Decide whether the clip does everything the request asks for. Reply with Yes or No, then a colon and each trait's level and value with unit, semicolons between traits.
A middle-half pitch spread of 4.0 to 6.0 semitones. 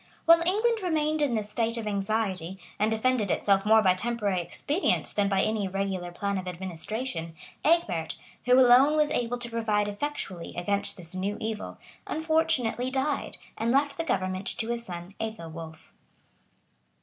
Yes: wide, 5.4 semitones